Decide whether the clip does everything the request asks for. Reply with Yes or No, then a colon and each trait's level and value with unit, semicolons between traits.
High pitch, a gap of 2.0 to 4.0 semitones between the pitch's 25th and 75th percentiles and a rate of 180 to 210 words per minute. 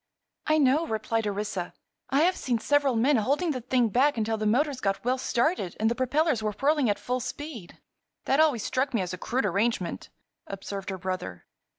No: high, 240 Hz; average, 5.2 semitones; average, 195 wpm